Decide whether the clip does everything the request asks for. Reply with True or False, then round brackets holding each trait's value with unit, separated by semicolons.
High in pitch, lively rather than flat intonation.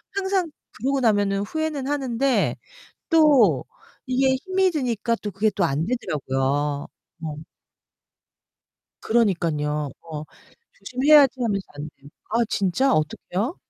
True (225 Hz; 8.8 semitones)